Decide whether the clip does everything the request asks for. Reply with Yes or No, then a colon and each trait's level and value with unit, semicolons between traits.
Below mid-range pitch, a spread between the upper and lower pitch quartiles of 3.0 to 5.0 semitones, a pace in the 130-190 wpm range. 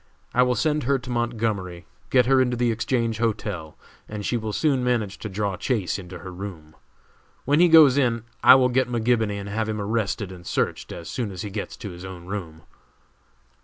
No: low, 110 Hz; average, 4.4 semitones; average, 200 wpm